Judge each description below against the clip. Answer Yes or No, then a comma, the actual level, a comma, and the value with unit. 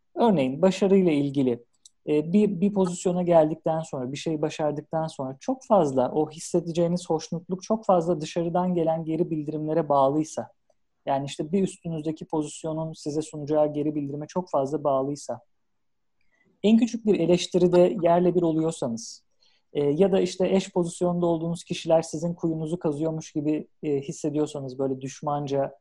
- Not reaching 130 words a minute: No, average, 135 wpm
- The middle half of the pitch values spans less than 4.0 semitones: Yes, average, 2.9 semitones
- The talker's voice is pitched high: No, medium, 160 Hz